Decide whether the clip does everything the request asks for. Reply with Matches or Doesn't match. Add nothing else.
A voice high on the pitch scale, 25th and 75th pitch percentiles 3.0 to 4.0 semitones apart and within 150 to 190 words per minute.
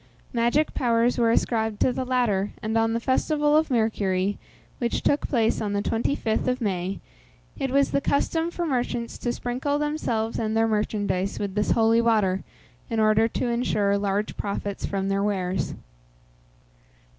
Matches